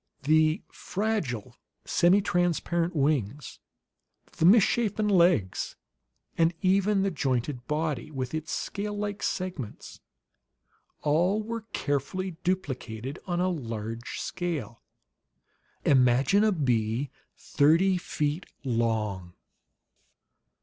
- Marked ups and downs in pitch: Yes, wide, 6.5 semitones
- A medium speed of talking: No, slow, 90 wpm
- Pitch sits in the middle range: Yes, medium, 155 Hz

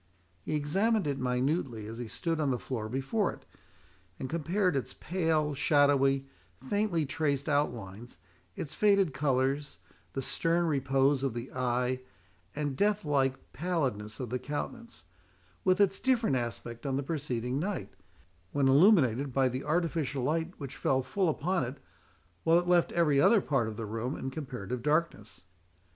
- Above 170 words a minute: No, average, 155 wpm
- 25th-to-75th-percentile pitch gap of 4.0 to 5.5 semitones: Yes, average, 4.5 semitones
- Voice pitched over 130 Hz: Yes, medium, 140 Hz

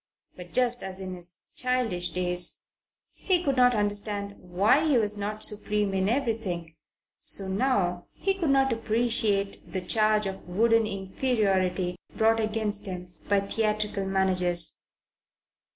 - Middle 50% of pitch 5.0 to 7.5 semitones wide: No, average, 3.3 semitones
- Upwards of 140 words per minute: No, slow, 135 wpm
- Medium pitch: No, high, 205 Hz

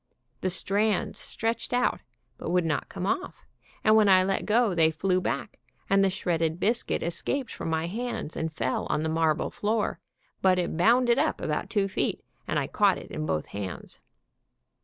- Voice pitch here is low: No, high, 190 Hz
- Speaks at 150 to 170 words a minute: No, average, 180 wpm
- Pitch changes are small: No, average, 5.2 semitones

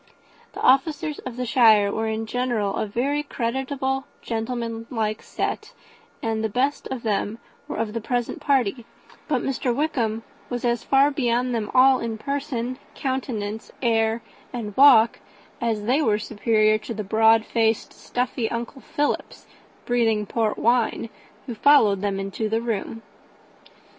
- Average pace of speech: Yes, average, 145 wpm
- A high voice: Yes, high, 230 Hz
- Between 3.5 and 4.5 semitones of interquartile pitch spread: No, narrow, 2.6 semitones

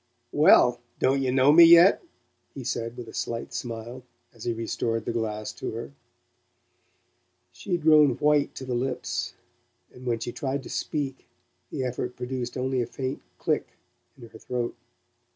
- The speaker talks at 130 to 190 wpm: Yes, average, 165 wpm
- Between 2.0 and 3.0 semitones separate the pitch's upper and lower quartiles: Yes, narrow, 2.6 semitones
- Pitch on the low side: Yes, low, 125 Hz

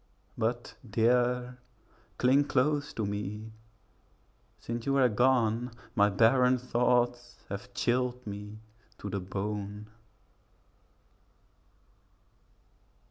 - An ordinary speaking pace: No, slow, 85 wpm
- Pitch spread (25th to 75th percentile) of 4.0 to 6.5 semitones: No, average, 3.1 semitones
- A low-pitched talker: Yes, low, 120 Hz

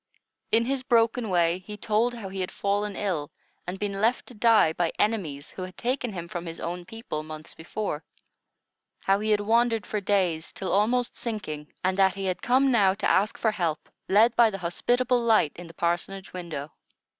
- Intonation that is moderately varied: Yes, average, 4.5 semitones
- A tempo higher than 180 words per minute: Yes, average, 195 wpm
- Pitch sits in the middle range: No, high, 200 Hz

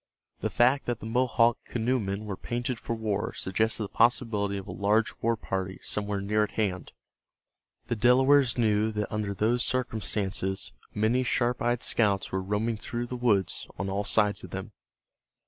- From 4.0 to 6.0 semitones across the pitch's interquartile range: No, average, 2.9 semitones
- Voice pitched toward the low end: Yes, low, 110 Hz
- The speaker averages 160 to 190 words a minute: Yes, average, 165 wpm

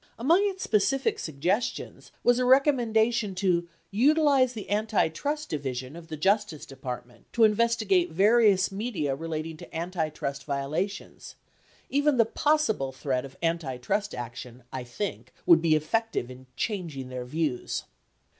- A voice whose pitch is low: No, medium, 180 Hz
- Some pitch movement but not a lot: No, wide, 8.5 semitones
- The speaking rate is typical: No, slow, 130 wpm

